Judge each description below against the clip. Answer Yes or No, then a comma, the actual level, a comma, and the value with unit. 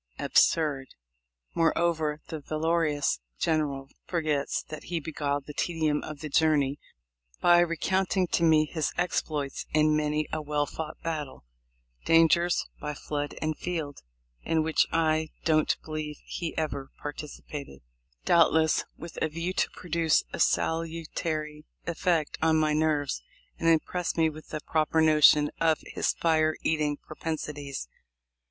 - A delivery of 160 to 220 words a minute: No, average, 140 wpm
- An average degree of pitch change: No, narrow, 1.6 semitones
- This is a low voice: No, medium, 155 Hz